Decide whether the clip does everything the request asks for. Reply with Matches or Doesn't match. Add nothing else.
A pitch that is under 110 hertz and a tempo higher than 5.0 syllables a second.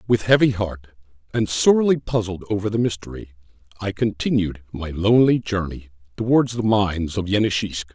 Matches